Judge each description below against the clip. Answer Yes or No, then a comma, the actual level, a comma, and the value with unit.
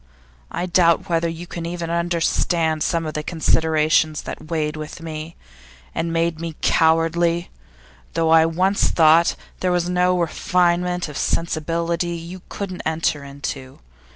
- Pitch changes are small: Yes, narrow, 1.4 semitones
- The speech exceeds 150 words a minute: No, average, 145 wpm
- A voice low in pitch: No, medium, 165 Hz